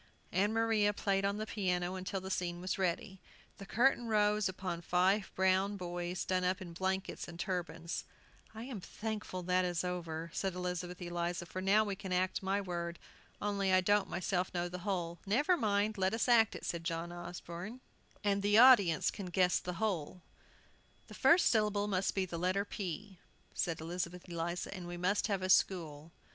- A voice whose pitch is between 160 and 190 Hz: Yes, medium, 185 Hz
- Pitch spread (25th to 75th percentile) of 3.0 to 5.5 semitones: No, narrow, 2.5 semitones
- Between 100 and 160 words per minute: No, average, 180 wpm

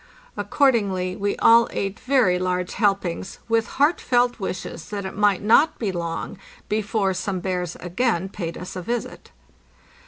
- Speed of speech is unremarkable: Yes, average, 145 wpm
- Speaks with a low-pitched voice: No, high, 195 Hz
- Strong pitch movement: No, average, 3.9 semitones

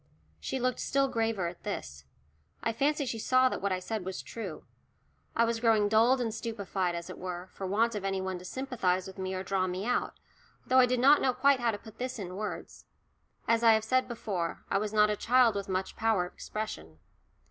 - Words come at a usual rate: No, fast, 225 wpm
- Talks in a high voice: Yes, high, 215 Hz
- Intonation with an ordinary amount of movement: Yes, average, 4.2 semitones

